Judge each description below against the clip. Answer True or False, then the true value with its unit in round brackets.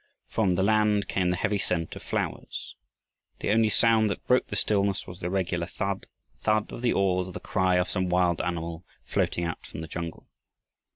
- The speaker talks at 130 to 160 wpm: False (195 wpm)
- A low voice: True (95 Hz)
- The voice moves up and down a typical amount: True (3.0 semitones)